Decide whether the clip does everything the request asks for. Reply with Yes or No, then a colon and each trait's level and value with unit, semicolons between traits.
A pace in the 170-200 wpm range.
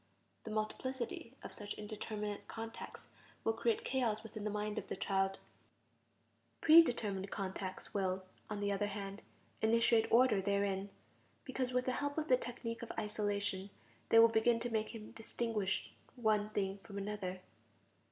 No: average, 150 wpm